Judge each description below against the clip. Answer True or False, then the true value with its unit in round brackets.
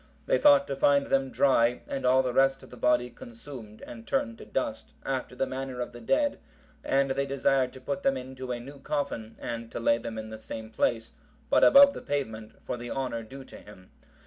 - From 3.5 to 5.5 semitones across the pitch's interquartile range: False (2.8 semitones)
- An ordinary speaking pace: False (220 wpm)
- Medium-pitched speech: False (130 Hz)